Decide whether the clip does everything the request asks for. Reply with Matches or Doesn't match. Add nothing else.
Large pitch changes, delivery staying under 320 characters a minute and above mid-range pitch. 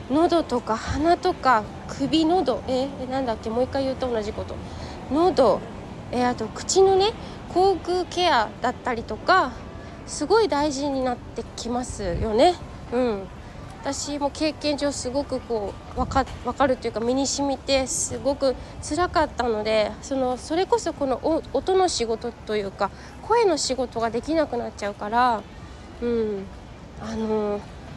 Doesn't match